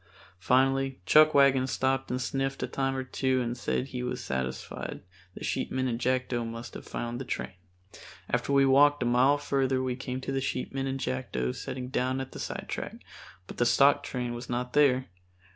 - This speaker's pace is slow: No, average, 185 wpm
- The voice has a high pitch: No, low, 130 Hz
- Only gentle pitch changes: Yes, narrow, 1.6 semitones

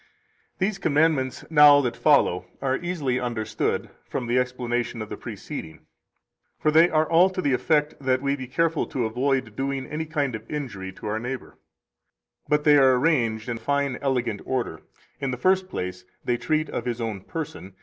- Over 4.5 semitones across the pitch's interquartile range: No, average, 4.1 semitones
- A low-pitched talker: Yes, low, 130 Hz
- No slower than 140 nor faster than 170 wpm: No, average, 180 wpm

